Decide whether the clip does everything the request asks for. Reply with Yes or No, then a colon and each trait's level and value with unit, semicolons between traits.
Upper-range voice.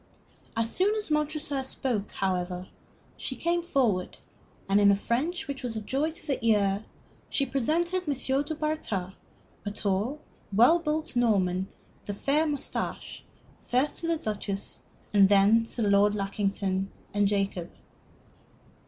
Yes: high, 230 Hz